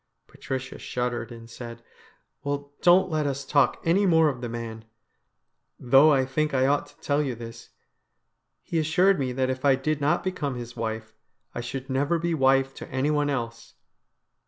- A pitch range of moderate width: Yes, average, 3.7 semitones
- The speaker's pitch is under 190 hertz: Yes, low, 135 Hz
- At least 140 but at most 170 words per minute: No, average, 180 wpm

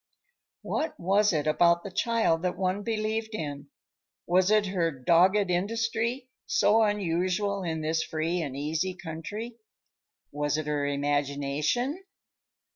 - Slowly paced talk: Yes, slow, 125 wpm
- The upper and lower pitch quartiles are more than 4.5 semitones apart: Yes, average, 5.2 semitones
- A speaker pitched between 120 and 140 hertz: No, medium, 180 Hz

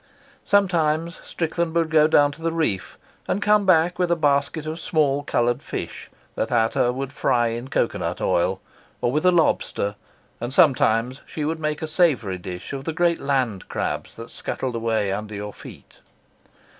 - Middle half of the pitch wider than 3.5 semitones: Yes, wide, 5.6 semitones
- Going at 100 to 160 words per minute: No, average, 175 wpm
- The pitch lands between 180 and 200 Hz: No, medium, 145 Hz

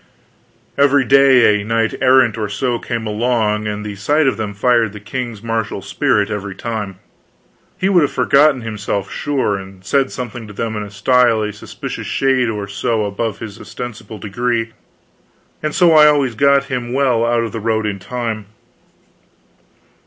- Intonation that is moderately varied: Yes, average, 3.5 semitones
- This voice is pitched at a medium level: No, low, 115 Hz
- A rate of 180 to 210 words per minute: No, average, 170 wpm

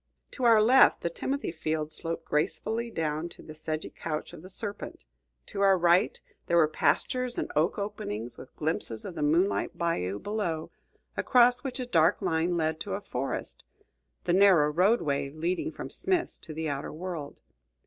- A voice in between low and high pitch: Yes, medium, 170 Hz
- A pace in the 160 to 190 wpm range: Yes, average, 170 wpm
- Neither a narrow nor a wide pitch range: Yes, average, 4.8 semitones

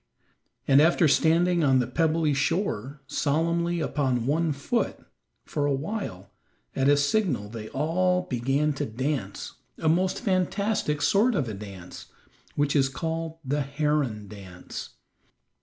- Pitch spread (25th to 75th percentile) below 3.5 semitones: No, average, 4.3 semitones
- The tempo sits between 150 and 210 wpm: No, slow, 135 wpm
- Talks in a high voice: No, medium, 150 Hz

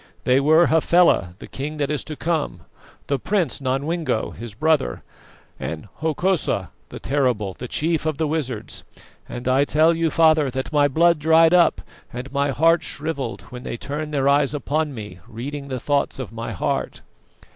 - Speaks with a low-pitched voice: No, medium, 145 Hz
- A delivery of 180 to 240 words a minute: No, average, 170 wpm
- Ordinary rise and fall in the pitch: Yes, average, 3.8 semitones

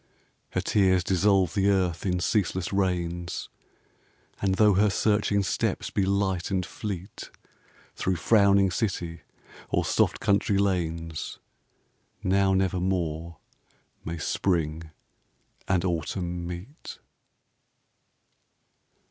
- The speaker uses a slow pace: Yes, slow, 100 wpm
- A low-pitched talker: Yes, very low, 95 Hz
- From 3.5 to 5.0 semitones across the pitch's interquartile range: No, narrow, 2.4 semitones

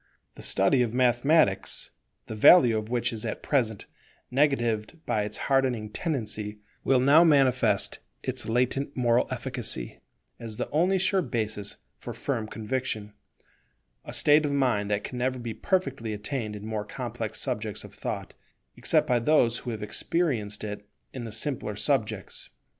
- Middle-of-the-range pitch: No, low, 120 Hz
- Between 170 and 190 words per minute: No, average, 155 wpm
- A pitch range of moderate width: Yes, average, 4.2 semitones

